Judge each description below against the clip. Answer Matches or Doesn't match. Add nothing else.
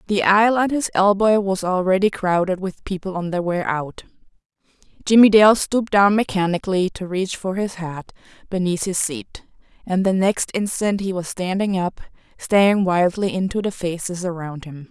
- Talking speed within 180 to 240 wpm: Doesn't match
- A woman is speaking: Matches